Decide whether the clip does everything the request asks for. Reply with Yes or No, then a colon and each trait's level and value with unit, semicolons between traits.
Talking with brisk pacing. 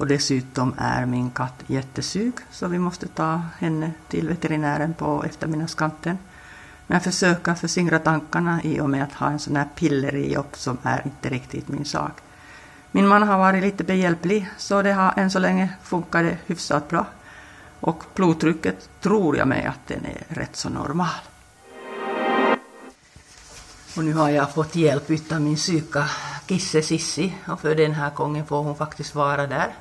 No: average, 165 wpm